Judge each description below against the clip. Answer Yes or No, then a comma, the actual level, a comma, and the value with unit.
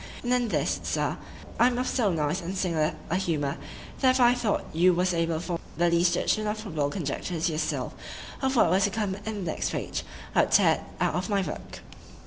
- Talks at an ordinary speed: No, fast, 225 wpm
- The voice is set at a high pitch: No, medium, 180 Hz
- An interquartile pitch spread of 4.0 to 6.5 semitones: Yes, average, 4.5 semitones